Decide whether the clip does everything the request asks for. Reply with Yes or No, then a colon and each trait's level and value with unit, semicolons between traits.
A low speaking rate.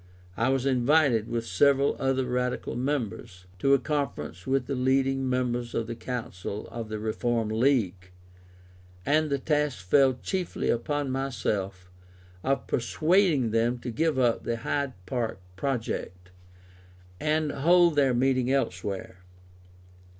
Yes: slow, 130 wpm